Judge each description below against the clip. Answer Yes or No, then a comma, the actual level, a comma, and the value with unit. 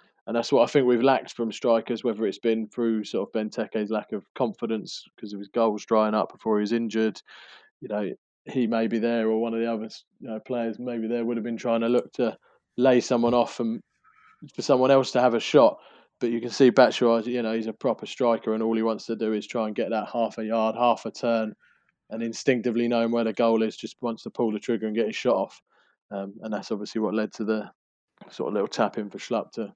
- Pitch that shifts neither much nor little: No, narrow, 1.2 semitones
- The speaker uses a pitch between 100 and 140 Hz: Yes, low, 115 Hz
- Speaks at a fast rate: Yes, fast, 255 wpm